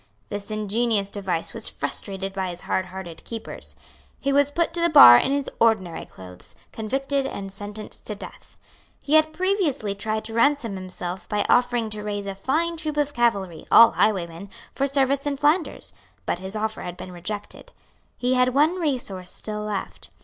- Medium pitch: No, high, 215 Hz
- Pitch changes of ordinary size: No, wide, 6.2 semitones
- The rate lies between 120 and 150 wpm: No, average, 170 wpm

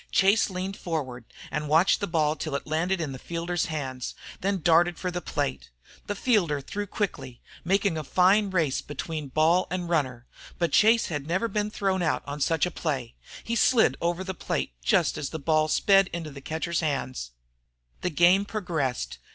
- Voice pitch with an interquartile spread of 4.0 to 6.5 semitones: Yes, average, 4.3 semitones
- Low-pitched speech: No, medium, 170 Hz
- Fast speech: No, average, 190 wpm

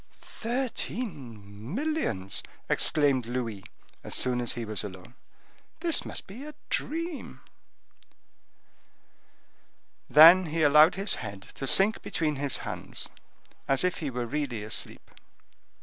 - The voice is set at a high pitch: No, medium, 145 Hz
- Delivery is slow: Yes, slow, 120 wpm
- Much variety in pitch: Yes, wide, 8.8 semitones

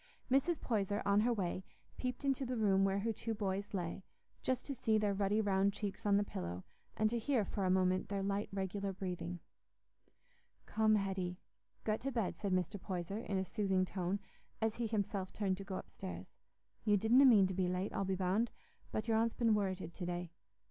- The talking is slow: No, average, 200 wpm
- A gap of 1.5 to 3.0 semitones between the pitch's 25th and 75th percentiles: Yes, average, 2.7 semitones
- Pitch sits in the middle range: No, high, 200 Hz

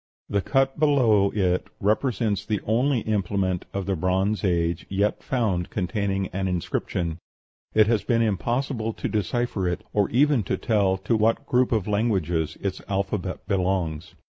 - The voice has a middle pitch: No, low, 100 Hz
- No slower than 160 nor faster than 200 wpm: No, average, 150 wpm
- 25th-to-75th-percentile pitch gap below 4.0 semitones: Yes, average, 3.4 semitones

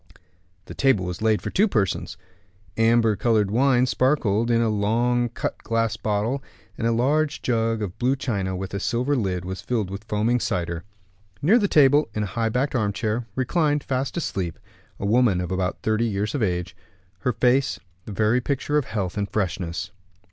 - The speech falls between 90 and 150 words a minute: No, average, 180 wpm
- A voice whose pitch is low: Yes, low, 115 Hz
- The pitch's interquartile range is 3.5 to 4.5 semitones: Yes, average, 4.1 semitones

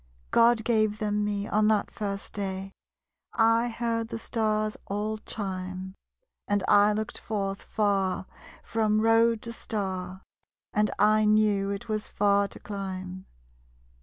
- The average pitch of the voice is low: No, high, 210 Hz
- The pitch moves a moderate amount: No, narrow, 1.7 semitones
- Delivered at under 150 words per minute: Yes, slow, 135 wpm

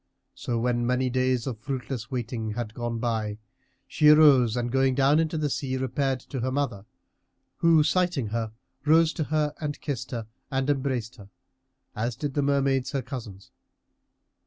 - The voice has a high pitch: No, low, 130 Hz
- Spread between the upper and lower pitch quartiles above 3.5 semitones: No, average, 3.2 semitones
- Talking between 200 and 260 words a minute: No, average, 165 wpm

